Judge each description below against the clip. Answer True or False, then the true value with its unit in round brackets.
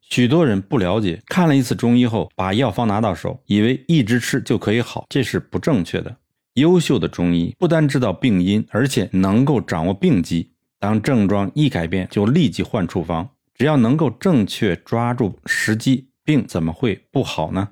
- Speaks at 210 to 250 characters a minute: False (280 characters per minute)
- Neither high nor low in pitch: False (110 Hz)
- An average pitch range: False (5.9 semitones)